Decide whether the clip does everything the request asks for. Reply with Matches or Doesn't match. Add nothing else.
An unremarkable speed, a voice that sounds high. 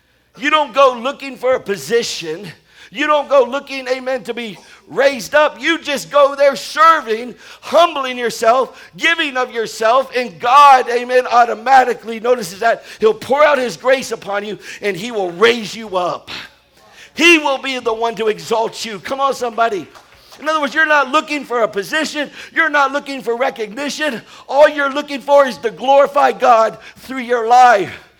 Matches